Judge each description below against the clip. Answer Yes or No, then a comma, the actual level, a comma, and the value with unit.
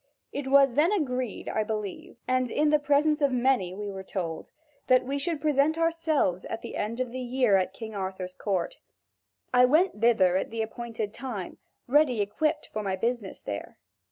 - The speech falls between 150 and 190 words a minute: Yes, average, 180 wpm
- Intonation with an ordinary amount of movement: No, wide, 5.9 semitones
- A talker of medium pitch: No, high, 245 Hz